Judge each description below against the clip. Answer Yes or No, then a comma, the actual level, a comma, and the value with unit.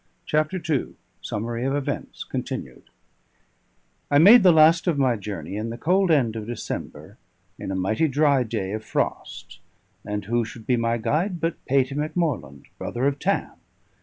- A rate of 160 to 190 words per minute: Yes, average, 165 wpm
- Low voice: Yes, low, 130 Hz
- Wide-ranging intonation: Yes, wide, 5.8 semitones